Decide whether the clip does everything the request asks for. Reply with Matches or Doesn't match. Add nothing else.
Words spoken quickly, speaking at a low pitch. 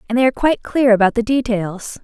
Doesn't match